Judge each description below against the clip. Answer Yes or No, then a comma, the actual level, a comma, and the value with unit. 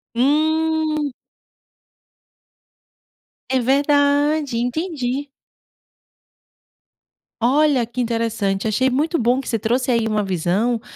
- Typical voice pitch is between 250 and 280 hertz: Yes, very high, 255 Hz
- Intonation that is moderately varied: Yes, average, 4.2 semitones